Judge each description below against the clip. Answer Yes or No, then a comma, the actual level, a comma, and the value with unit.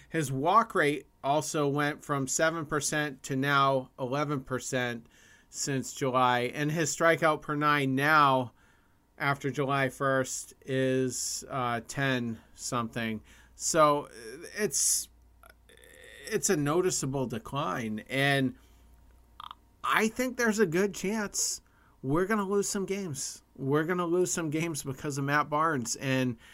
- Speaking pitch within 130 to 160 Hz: Yes, medium, 140 Hz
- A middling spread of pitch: Yes, average, 4.3 semitones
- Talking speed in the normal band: No, slow, 120 wpm